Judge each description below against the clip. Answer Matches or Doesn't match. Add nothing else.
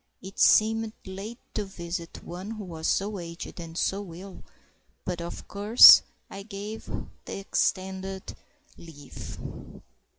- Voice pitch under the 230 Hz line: Matches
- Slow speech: Matches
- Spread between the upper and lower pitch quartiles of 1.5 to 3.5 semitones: Matches